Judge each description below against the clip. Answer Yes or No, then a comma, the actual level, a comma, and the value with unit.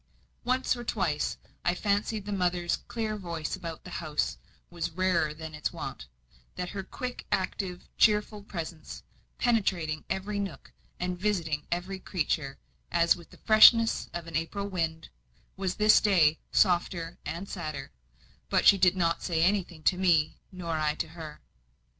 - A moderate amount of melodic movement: Yes, average, 3.6 semitones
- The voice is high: No, medium, 180 Hz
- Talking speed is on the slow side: No, average, 155 wpm